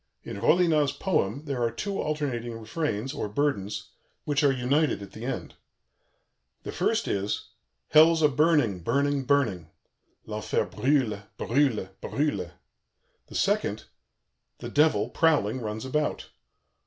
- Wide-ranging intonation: Yes, wide, 5.8 semitones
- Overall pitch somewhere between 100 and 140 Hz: Yes, low, 135 Hz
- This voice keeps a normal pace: No, slow, 125 wpm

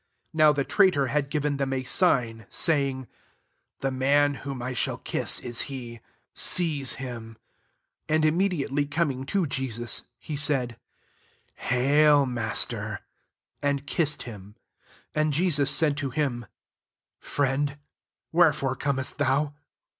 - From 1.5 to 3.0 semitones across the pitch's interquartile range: Yes, average, 2.7 semitones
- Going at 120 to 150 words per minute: Yes, average, 140 wpm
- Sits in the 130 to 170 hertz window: Yes, medium, 140 Hz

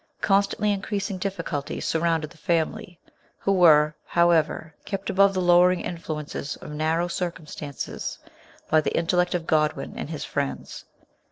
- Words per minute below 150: Yes, average, 140 wpm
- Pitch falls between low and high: Yes, medium, 170 Hz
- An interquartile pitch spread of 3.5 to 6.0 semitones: No, average, 2.9 semitones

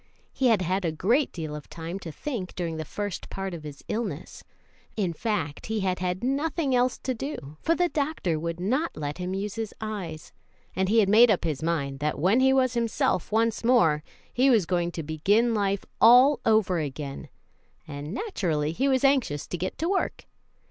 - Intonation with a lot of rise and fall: Yes, wide, 6.8 semitones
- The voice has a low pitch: No, high, 195 Hz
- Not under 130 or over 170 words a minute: No, average, 195 wpm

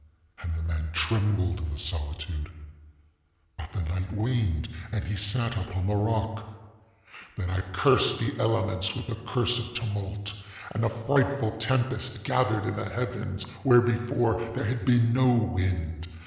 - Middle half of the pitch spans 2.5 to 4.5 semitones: No, average, 4.9 semitones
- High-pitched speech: No, low, 105 Hz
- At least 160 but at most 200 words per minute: No, average, 150 wpm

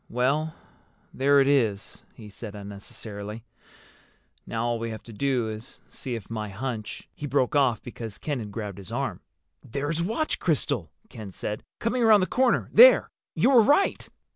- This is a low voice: Yes, low, 120 Hz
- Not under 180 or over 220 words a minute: No, average, 165 wpm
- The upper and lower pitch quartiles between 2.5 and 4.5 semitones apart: No, wide, 5.5 semitones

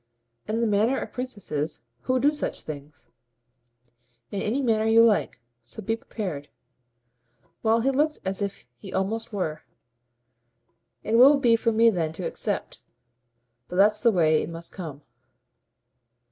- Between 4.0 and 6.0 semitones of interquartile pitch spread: Yes, wide, 5.6 semitones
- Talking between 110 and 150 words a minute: Yes, average, 145 wpm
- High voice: Yes, high, 215 Hz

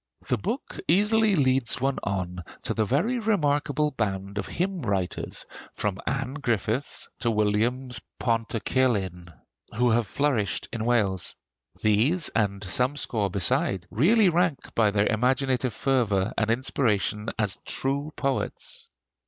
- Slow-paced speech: Yes, slow, 130 wpm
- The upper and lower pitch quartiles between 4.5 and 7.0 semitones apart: Yes, average, 5.3 semitones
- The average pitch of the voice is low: Yes, low, 120 Hz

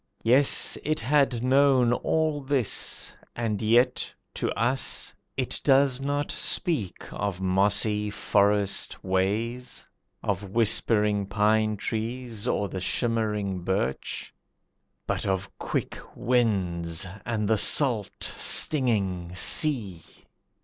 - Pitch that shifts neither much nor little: Yes, average, 4.3 semitones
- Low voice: Yes, low, 110 Hz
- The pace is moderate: No, slow, 100 wpm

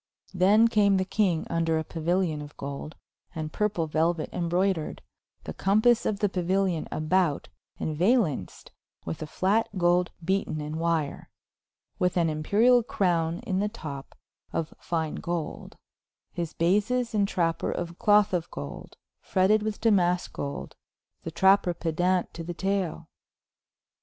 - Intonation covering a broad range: No, average, 3.5 semitones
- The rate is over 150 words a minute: No, average, 140 wpm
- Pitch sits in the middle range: Yes, medium, 175 Hz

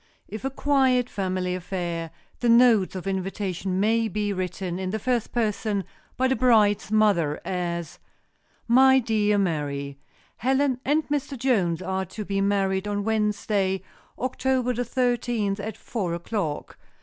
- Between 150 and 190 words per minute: No, average, 140 wpm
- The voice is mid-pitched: No, high, 205 Hz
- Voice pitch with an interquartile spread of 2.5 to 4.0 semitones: No, average, 4.5 semitones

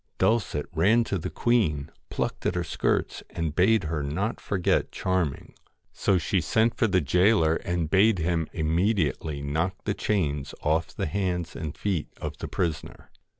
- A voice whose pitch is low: Yes, very low, 85 Hz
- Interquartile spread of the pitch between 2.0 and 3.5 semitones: No, average, 4.1 semitones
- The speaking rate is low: No, average, 160 wpm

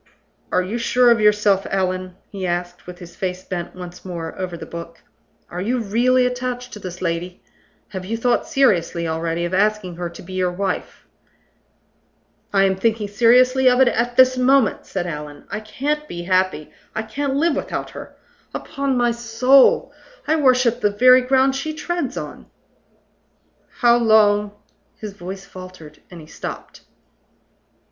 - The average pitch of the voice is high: Yes, high, 210 Hz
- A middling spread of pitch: No, wide, 5.7 semitones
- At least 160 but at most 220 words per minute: Yes, average, 165 wpm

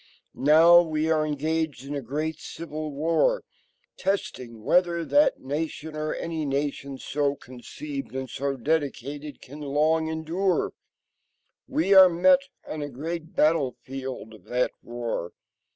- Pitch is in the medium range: Yes, medium, 155 Hz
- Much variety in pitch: No, average, 3.2 semitones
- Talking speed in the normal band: No, slow, 130 wpm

